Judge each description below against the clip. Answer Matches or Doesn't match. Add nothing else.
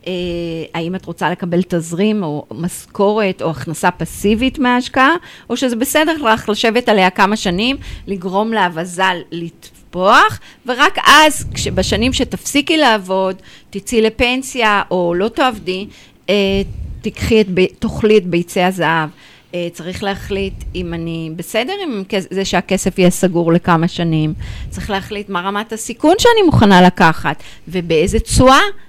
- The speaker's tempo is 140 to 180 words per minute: Doesn't match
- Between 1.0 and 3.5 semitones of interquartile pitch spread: Doesn't match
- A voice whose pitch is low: Doesn't match